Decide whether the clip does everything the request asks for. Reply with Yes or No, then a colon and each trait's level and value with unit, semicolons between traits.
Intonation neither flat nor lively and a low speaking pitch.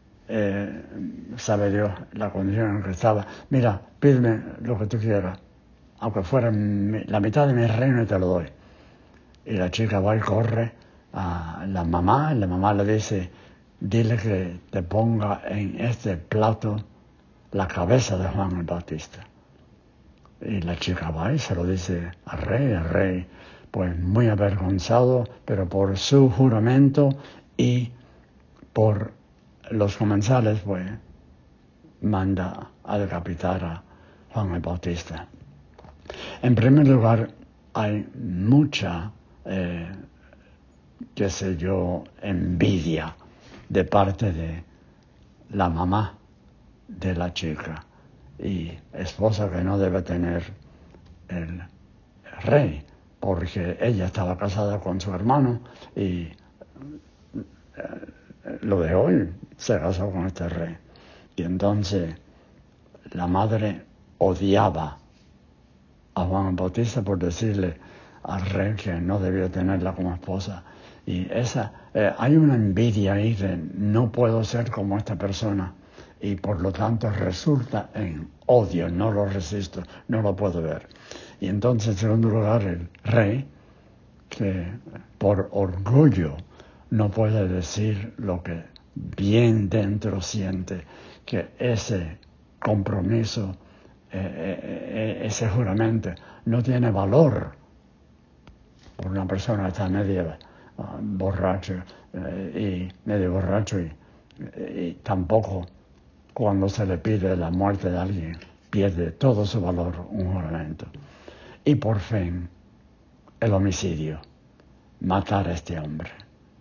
Yes: average, 3.5 semitones; very low, 95 Hz